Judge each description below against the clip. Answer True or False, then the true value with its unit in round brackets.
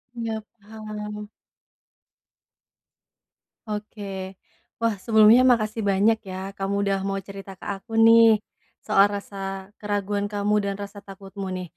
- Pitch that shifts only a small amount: True (1.7 semitones)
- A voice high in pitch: True (205 Hz)